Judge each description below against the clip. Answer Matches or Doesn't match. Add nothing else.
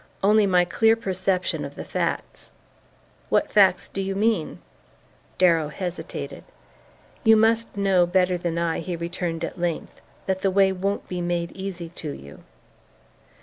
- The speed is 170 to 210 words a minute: Doesn't match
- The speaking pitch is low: Doesn't match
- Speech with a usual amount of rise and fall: Doesn't match